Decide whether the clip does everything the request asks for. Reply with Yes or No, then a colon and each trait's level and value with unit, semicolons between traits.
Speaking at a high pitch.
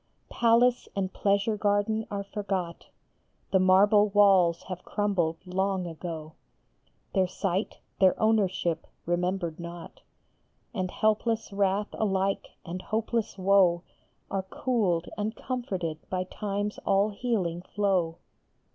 Yes: high, 195 Hz